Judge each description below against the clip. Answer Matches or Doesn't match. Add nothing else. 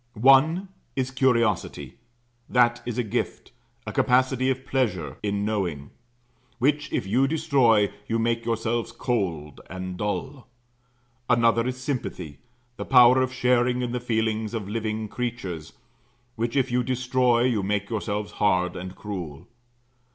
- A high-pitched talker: Doesn't match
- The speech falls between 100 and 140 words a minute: Matches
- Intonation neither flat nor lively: Matches